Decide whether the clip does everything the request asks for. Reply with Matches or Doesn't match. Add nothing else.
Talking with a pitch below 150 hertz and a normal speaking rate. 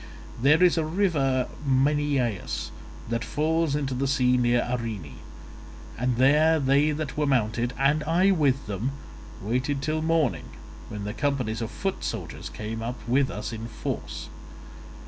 Matches